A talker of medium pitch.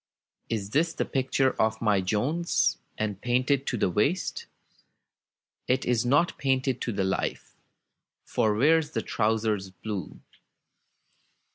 No: low, 120 Hz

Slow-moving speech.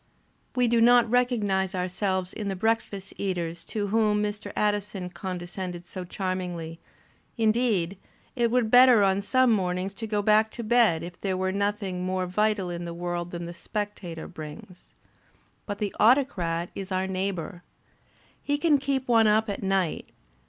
No: average, 160 wpm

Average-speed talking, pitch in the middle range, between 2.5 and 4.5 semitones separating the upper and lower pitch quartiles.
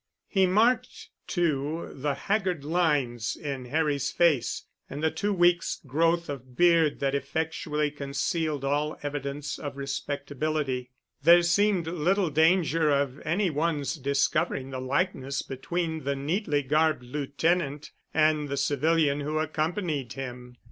No: slow, 125 wpm; medium, 150 Hz; average, 3.2 semitones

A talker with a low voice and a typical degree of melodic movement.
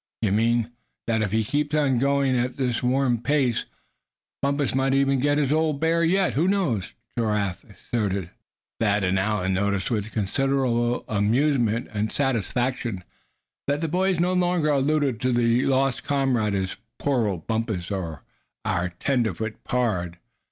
Yes: low, 120 Hz; average, 4.9 semitones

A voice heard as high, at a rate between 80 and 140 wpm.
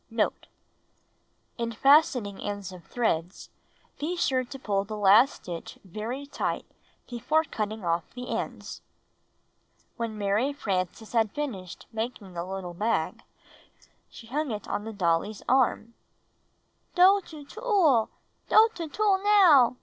Yes: high, 230 Hz; slow, 135 wpm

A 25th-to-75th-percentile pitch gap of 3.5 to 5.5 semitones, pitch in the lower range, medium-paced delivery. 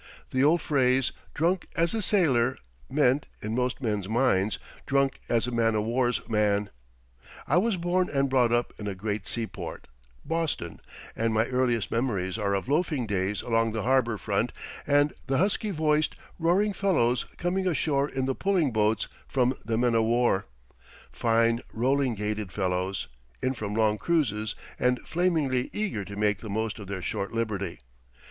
Yes: average, 5.1 semitones; low, 120 Hz; average, 165 wpm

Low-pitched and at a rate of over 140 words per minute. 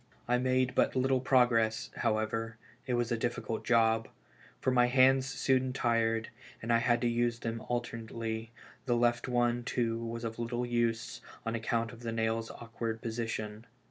Yes: low, 115 Hz; average, 165 wpm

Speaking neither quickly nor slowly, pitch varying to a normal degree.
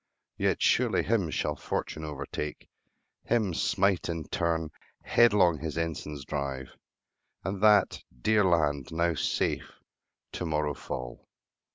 No: slow, 120 wpm; average, 4.3 semitones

